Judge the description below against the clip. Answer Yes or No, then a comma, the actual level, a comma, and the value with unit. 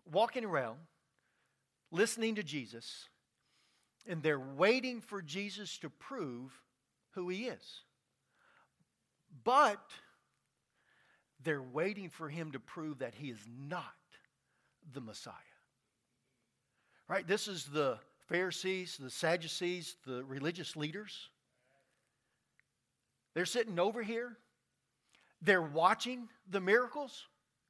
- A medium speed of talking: No, slow, 100 wpm